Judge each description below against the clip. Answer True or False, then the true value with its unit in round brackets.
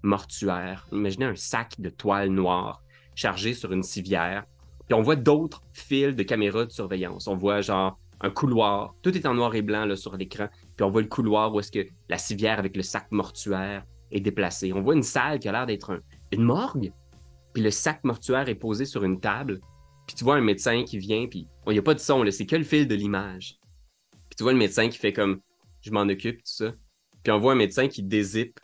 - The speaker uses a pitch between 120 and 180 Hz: False (100 Hz)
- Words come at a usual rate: False (235 wpm)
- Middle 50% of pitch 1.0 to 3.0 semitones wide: False (3.4 semitones)